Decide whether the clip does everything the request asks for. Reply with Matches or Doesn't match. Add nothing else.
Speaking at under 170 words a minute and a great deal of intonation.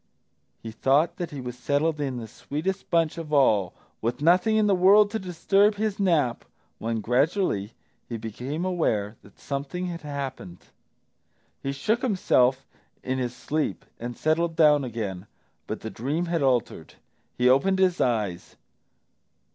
Matches